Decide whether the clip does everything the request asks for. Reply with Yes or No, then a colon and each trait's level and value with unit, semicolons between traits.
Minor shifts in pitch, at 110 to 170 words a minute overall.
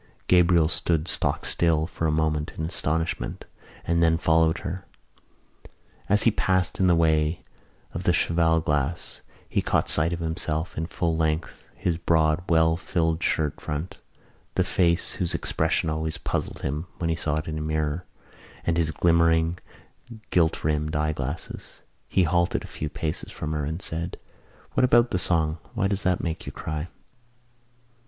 Yes: narrow, 1.7 semitones; average, 160 wpm